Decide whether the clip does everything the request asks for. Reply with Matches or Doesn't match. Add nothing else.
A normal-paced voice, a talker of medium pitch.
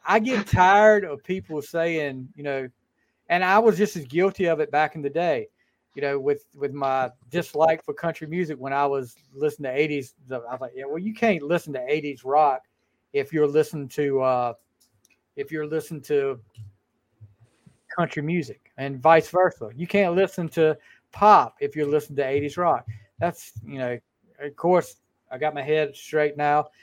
Matches